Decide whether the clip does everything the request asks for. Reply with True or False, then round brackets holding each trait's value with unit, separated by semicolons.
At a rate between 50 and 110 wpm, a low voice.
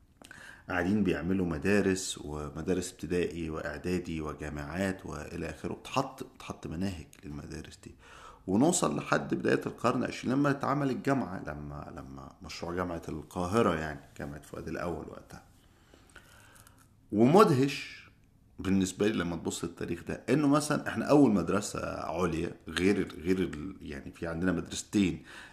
False (120 wpm; 90 Hz)